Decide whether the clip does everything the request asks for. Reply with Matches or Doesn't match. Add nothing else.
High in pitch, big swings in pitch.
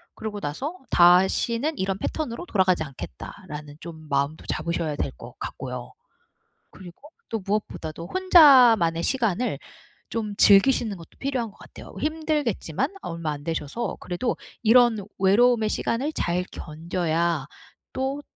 Matches